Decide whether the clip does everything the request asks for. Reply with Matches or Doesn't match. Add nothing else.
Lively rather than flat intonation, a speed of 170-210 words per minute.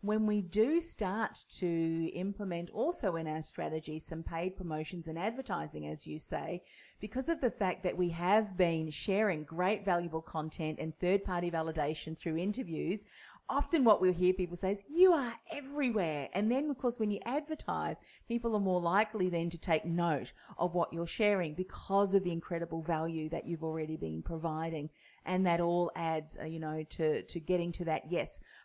Doesn't match